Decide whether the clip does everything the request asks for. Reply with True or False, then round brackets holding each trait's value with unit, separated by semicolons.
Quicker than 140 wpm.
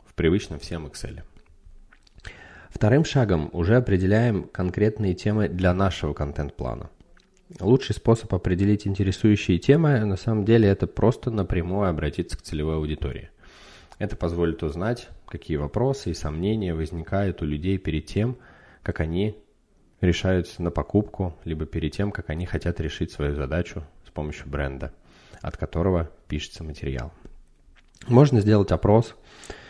False (125 wpm)